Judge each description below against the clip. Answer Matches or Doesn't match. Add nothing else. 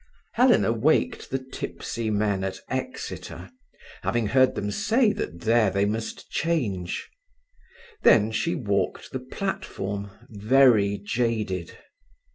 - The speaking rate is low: Matches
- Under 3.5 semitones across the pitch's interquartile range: Doesn't match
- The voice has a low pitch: Matches